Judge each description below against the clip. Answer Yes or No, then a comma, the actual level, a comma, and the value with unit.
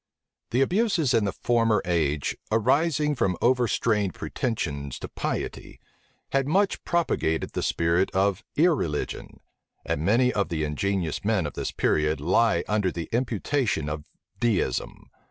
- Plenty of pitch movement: Yes, wide, 7.5 semitones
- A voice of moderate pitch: No, low, 105 Hz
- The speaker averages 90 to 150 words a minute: Yes, slow, 135 wpm